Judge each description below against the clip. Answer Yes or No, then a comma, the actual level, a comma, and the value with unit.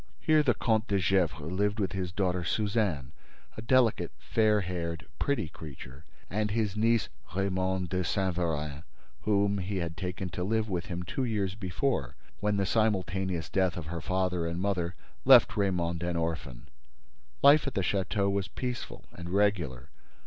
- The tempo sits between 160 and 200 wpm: Yes, average, 165 wpm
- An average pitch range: Yes, average, 3.3 semitones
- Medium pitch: No, very low, 95 Hz